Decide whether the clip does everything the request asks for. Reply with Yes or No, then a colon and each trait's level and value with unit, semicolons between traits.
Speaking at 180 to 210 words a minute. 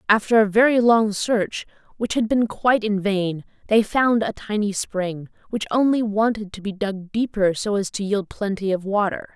Yes: average, 190 wpm